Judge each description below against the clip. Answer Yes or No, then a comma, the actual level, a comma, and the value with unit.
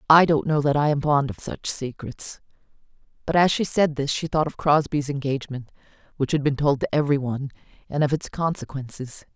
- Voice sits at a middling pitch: Yes, medium, 145 Hz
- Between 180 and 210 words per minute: Yes, average, 200 wpm